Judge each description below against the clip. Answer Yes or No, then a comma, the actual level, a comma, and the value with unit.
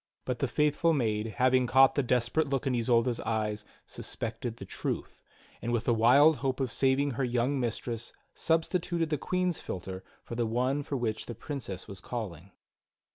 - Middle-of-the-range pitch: No, low, 125 Hz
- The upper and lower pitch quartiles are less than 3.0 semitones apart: No, average, 3.6 semitones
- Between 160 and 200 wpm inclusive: Yes, average, 175 wpm